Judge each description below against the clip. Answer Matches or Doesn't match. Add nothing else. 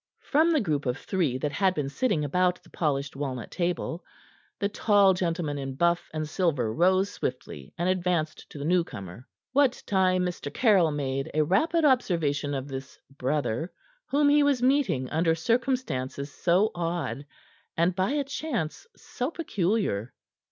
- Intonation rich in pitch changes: Matches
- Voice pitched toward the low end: Doesn't match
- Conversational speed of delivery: Matches